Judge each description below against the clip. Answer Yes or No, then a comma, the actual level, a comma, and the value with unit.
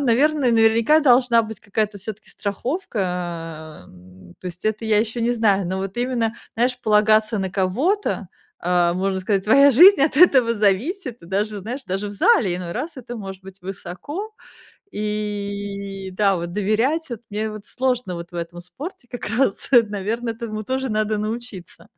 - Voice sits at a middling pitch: No, high, 215 Hz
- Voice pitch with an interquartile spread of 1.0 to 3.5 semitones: No, average, 4.1 semitones